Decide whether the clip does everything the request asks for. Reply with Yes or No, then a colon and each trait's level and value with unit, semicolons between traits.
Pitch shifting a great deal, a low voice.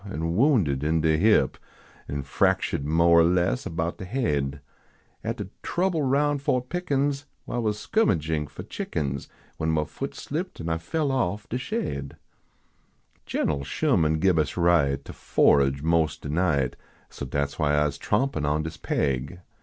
Yes: wide, 8.7 semitones; very low, 80 Hz